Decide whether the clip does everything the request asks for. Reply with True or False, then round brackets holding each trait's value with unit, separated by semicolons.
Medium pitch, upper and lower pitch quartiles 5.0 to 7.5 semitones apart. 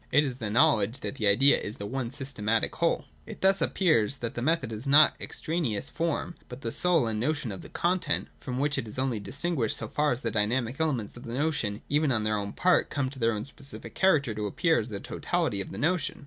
False (130 Hz; 5.4 semitones)